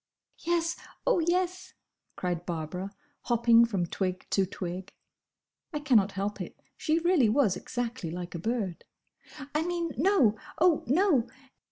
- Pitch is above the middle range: Yes, high, 235 Hz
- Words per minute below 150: Yes, slow, 135 wpm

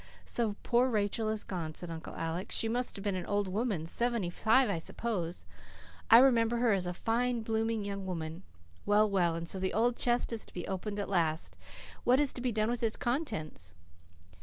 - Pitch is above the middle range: Yes, high, 210 Hz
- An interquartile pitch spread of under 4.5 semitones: No, average, 4.8 semitones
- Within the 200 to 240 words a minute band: Yes, fast, 205 wpm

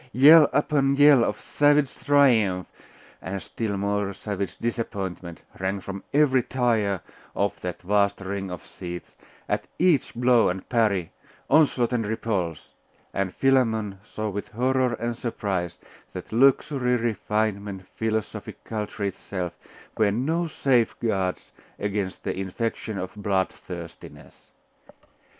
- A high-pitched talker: No, low, 110 Hz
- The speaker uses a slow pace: Yes, slow, 120 wpm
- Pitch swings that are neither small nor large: Yes, average, 4.3 semitones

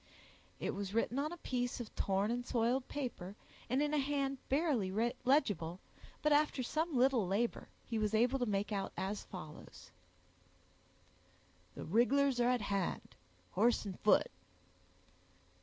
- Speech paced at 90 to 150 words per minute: Yes, average, 145 wpm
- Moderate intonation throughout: Yes, average, 5.0 semitones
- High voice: Yes, high, 240 Hz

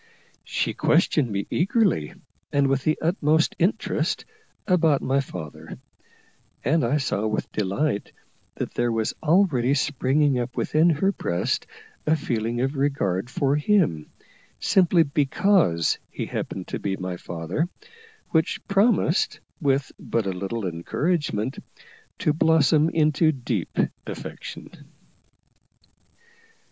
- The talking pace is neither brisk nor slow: No, slow, 115 wpm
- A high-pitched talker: No, medium, 140 Hz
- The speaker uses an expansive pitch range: Yes, wide, 6.3 semitones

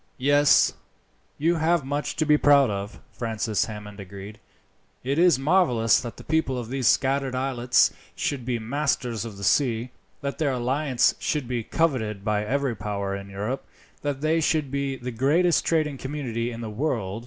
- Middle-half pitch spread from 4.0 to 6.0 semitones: Yes, average, 4.5 semitones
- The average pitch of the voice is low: Yes, low, 130 Hz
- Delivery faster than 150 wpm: Yes, average, 170 wpm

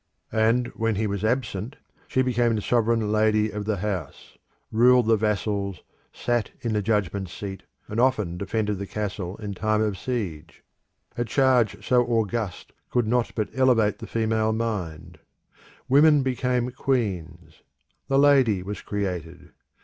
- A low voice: Yes, low, 110 Hz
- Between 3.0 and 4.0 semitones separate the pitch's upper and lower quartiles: Yes, average, 3.4 semitones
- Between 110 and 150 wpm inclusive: Yes, average, 145 wpm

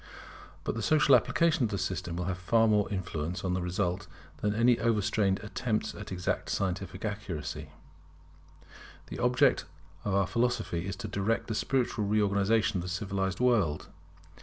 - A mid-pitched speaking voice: No, low, 100 Hz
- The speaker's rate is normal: Yes, average, 160 wpm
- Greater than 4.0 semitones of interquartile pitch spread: No, average, 3.3 semitones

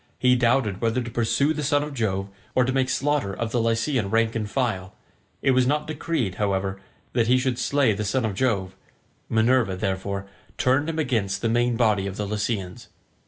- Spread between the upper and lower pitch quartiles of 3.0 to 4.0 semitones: No, average, 4.5 semitones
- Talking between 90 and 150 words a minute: No, average, 195 wpm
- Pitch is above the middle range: No, low, 115 Hz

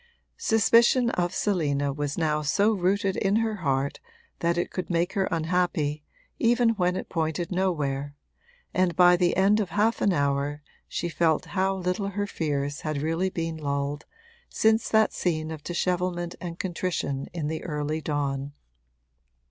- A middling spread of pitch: Yes, average, 4.2 semitones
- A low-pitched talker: No, medium, 175 Hz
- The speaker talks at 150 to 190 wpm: Yes, average, 155 wpm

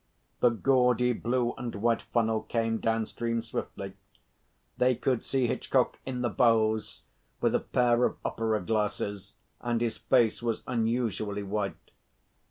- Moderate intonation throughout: No, narrow, 2.0 semitones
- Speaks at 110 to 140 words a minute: Yes, slow, 135 wpm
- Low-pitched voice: Yes, low, 115 Hz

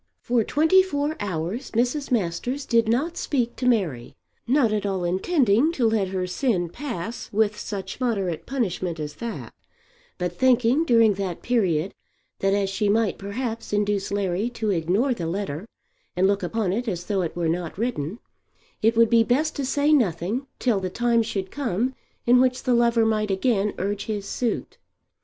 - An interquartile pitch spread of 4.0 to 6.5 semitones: Yes, average, 4.4 semitones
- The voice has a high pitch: Yes, high, 215 Hz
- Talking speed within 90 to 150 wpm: No, average, 175 wpm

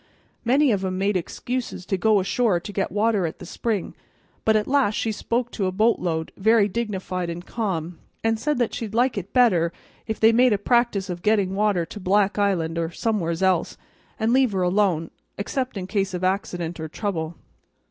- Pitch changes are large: No, average, 3.7 semitones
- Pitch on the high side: Yes, high, 200 Hz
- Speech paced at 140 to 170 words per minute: No, average, 200 wpm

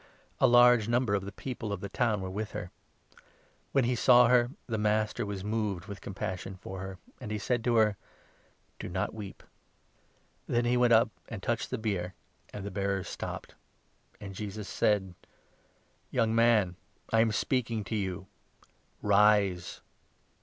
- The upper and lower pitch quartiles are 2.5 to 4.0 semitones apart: Yes, average, 3.1 semitones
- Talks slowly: No, average, 175 wpm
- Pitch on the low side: Yes, low, 105 Hz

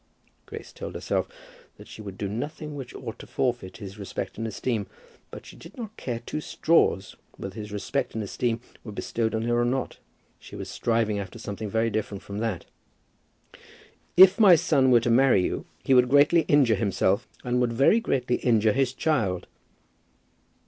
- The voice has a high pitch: No, low, 115 Hz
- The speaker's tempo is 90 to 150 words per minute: No, average, 185 wpm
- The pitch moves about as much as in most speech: Yes, average, 4.1 semitones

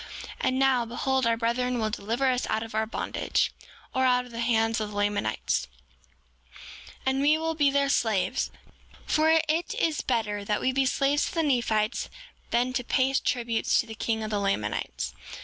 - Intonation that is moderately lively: Yes, average, 3.4 semitones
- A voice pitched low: No, high, 240 Hz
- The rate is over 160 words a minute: Yes, average, 185 wpm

